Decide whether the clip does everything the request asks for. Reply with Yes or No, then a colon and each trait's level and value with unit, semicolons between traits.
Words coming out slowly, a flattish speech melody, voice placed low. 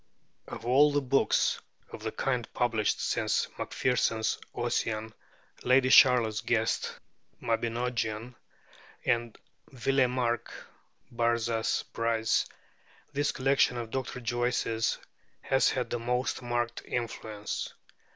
Yes: slow, 100 wpm; narrow, 1.9 semitones; low, 120 Hz